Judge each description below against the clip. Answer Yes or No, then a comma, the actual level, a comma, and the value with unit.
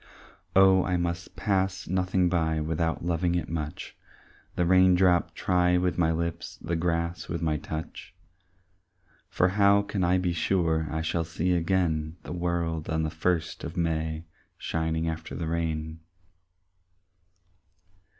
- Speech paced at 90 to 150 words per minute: Yes, average, 140 wpm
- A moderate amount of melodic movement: No, narrow, 1.9 semitones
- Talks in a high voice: No, very low, 85 Hz